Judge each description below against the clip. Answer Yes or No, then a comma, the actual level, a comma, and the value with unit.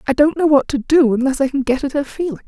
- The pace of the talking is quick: Yes, fast, 315 wpm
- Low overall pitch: No, very high, 280 Hz